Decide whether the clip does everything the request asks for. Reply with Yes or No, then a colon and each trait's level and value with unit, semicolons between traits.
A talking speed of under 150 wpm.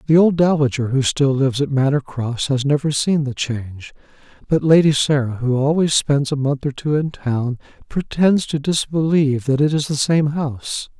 No: average, 190 wpm